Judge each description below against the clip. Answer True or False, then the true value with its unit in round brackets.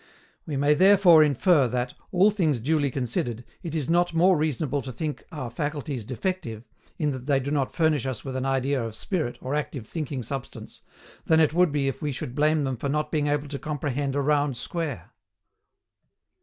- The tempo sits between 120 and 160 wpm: False (195 wpm)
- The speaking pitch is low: False (145 Hz)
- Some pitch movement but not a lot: True (3.1 semitones)